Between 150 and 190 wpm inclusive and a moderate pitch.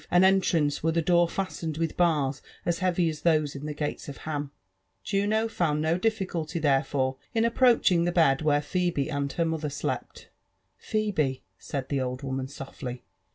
Yes: average, 170 wpm; medium, 160 Hz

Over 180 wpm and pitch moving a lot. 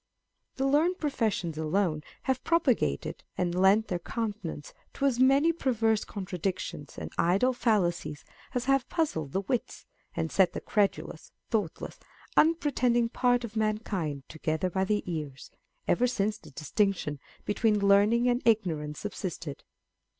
No: slow, 135 wpm; wide, 6.1 semitones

